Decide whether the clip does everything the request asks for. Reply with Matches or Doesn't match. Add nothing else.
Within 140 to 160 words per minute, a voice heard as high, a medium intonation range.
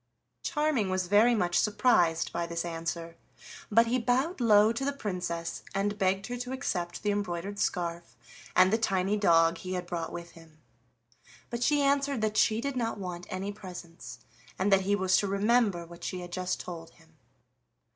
Doesn't match